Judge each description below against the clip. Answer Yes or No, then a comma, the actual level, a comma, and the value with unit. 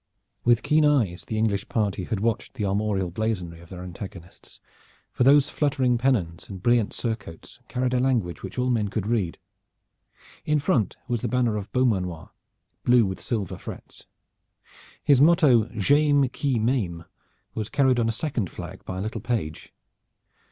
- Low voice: Yes, low, 115 Hz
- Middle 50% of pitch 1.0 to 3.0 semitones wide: No, average, 4.8 semitones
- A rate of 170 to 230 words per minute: No, average, 160 wpm